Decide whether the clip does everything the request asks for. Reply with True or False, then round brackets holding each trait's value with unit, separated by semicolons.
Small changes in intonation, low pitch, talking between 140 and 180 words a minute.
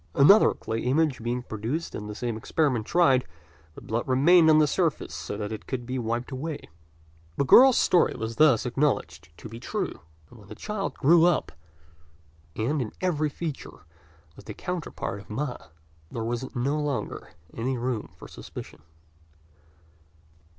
False (5.0 semitones; 130 Hz; 160 wpm)